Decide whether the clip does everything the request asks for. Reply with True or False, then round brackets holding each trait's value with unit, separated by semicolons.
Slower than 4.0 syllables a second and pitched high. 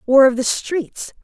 True (3.8 syllables/s; 270 Hz)